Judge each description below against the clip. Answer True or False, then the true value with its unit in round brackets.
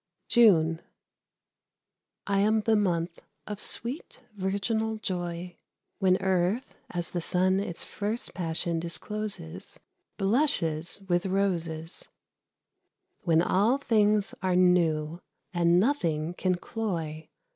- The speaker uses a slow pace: True (105 wpm)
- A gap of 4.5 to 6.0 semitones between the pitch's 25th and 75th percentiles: False (3.7 semitones)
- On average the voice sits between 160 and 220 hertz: True (185 Hz)